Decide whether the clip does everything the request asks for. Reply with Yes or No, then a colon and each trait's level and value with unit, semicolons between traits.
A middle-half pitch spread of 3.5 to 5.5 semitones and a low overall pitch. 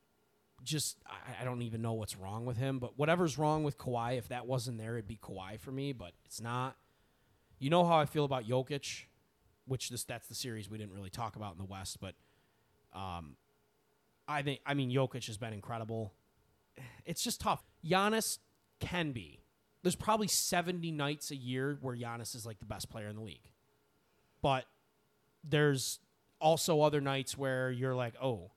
Yes: average, 4.4 semitones; low, 125 Hz